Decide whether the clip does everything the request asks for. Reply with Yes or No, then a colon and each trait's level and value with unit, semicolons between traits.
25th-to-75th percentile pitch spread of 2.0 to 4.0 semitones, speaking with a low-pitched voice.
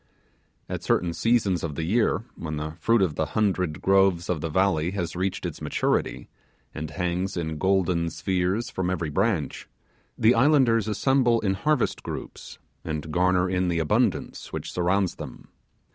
Yes: average, 3.5 semitones; very low, 90 Hz